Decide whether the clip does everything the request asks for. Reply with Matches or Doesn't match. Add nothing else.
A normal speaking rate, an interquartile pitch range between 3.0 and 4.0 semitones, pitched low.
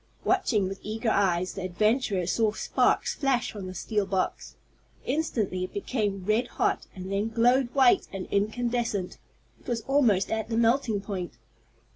Doesn't match